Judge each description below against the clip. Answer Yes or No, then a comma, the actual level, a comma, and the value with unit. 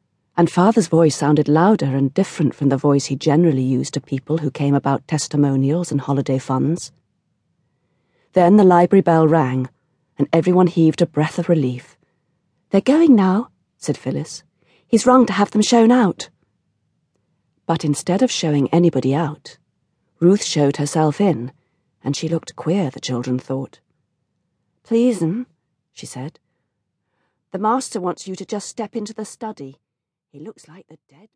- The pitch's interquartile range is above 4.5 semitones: Yes, average, 5.2 semitones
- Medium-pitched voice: Yes, medium, 160 Hz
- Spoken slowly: No, average, 155 wpm